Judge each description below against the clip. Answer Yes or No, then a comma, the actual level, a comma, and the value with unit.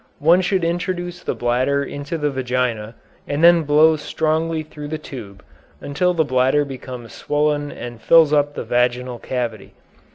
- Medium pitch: Yes, medium, 145 Hz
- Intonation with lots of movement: No, average, 4.1 semitones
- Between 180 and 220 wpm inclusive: No, average, 155 wpm